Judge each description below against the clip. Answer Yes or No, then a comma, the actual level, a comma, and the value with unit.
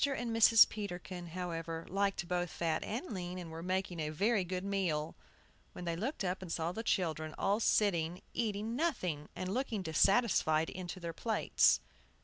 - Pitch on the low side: No, medium, 180 Hz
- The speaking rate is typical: Yes, average, 165 wpm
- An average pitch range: Yes, average, 3.9 semitones